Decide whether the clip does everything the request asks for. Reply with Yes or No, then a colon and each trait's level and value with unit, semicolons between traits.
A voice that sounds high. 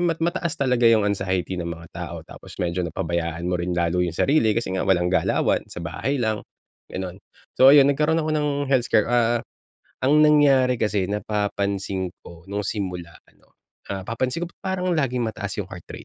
No: low, 105 Hz